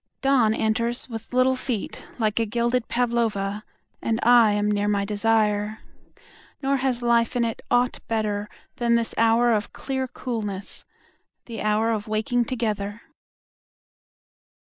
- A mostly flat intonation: Yes, narrow, 2.3 semitones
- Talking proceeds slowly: Yes, slow, 115 wpm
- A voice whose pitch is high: Yes, high, 225 Hz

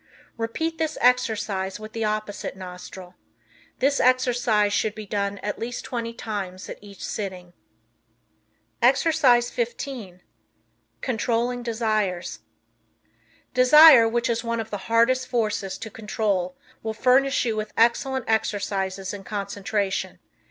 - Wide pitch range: No, average, 3.3 semitones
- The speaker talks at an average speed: No, slow, 120 wpm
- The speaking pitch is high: Yes, high, 220 Hz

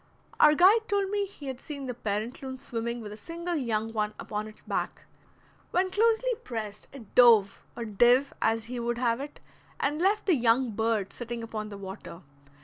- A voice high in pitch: Yes, high, 240 Hz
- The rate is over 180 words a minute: Yes, average, 190 wpm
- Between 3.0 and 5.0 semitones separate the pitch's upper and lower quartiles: No, wide, 5.5 semitones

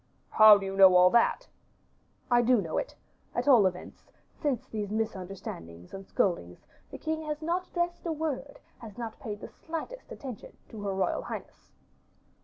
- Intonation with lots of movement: Yes, wide, 7.2 semitones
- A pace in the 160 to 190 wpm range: Yes, average, 170 wpm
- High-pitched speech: Yes, high, 220 Hz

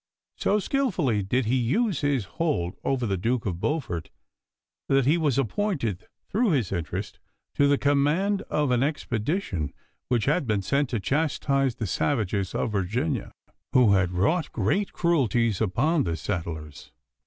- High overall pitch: No, low, 125 Hz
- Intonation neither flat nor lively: No, wide, 7.2 semitones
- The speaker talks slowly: No, average, 150 wpm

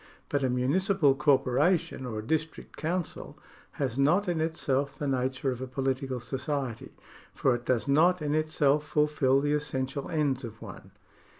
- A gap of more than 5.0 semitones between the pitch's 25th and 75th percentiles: No, average, 2.7 semitones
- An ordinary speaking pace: Yes, average, 160 wpm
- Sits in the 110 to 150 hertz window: Yes, medium, 140 Hz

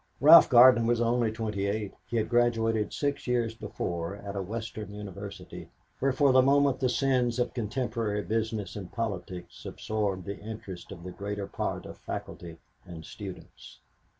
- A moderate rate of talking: Yes, average, 155 wpm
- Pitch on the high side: No, low, 110 Hz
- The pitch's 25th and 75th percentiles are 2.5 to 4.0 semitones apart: Yes, average, 3.3 semitones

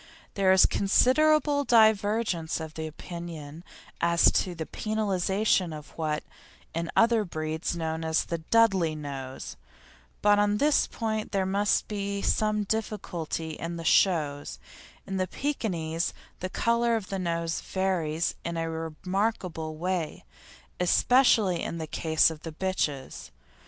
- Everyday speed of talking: No, slow, 130 wpm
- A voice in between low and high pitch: Yes, medium, 180 Hz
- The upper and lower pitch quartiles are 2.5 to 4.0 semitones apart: No, average, 4.6 semitones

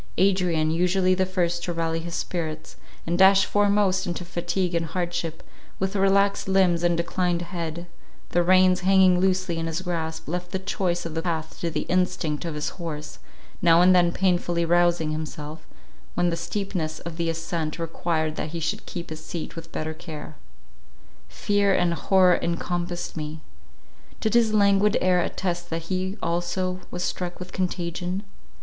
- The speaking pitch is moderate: Yes, medium, 175 Hz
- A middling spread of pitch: No, narrow, 2.1 semitones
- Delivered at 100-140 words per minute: No, average, 165 wpm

